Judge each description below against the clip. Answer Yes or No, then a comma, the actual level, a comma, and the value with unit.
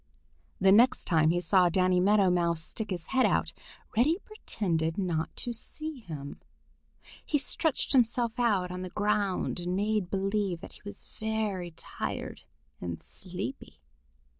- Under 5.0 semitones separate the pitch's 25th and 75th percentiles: Yes, average, 3.9 semitones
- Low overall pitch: No, high, 195 Hz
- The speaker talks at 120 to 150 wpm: Yes, average, 145 wpm